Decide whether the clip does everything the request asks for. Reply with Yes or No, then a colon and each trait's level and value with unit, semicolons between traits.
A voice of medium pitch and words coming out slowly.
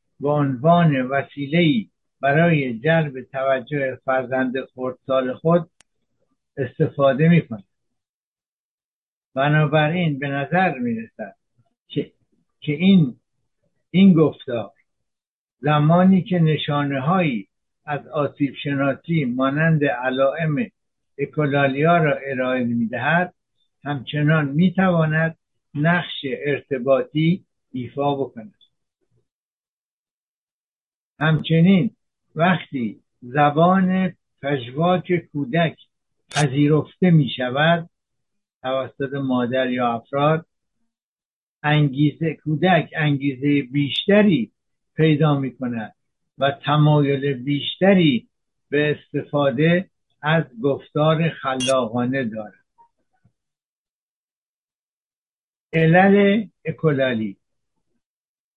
Yes: medium, 145 Hz; slow, 75 wpm